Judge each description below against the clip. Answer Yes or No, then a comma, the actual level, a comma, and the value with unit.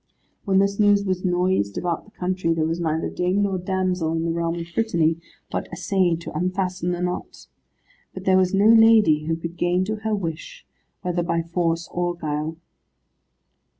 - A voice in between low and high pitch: Yes, medium, 180 Hz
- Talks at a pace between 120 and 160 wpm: No, average, 180 wpm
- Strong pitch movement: No, narrow, 2.5 semitones